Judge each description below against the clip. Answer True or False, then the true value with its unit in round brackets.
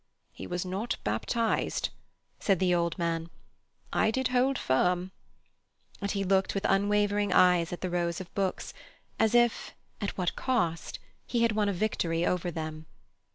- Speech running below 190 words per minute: True (150 wpm)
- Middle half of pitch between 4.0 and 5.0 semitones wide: False (3.3 semitones)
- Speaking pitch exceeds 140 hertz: True (185 Hz)